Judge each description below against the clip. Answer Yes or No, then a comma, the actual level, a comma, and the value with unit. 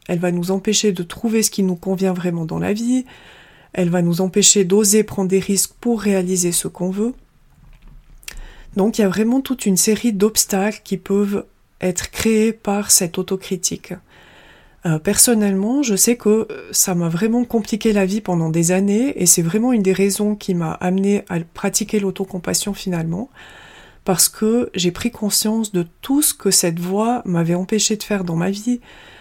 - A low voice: No, high, 200 Hz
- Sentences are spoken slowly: No, average, 180 wpm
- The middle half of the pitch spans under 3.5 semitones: Yes, average, 2.8 semitones